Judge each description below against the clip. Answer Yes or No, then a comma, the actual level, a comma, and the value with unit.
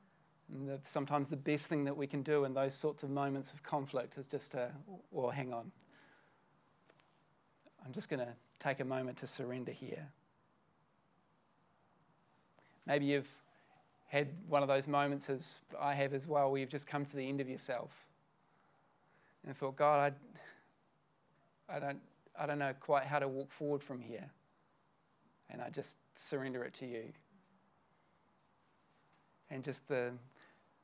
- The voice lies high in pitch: No, medium, 140 Hz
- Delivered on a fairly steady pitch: Yes, narrow, 1.5 semitones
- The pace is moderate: Yes, average, 155 wpm